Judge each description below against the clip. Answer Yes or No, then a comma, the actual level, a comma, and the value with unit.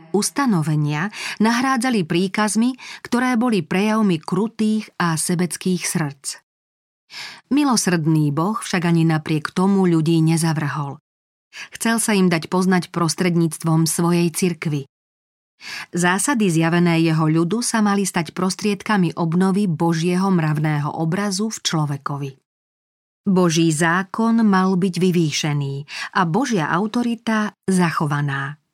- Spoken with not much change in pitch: No, average, 4.1 semitones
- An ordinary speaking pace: No, slow, 100 wpm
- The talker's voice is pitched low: No, medium, 175 Hz